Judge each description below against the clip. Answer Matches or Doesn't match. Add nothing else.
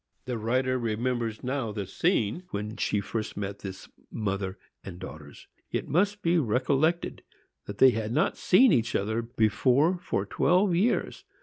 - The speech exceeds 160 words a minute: Doesn't match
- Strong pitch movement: Matches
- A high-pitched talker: Doesn't match